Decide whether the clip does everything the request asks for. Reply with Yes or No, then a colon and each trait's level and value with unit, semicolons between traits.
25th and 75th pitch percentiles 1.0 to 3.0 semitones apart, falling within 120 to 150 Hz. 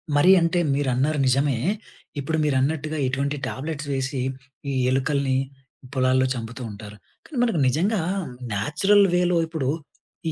No: average, 3.6 semitones; medium, 140 Hz